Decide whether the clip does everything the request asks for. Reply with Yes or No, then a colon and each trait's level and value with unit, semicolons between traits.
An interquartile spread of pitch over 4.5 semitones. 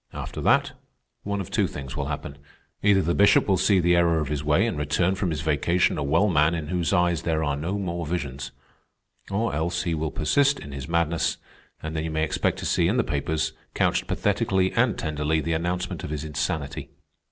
No: average, 3.1 semitones